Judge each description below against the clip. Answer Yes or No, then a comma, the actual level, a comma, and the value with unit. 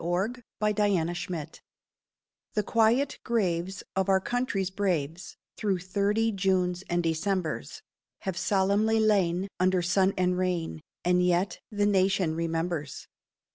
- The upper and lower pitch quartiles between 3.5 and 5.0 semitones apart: No, average, 2.7 semitones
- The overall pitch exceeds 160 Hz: Yes, medium, 185 Hz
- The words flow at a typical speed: No, slow, 115 wpm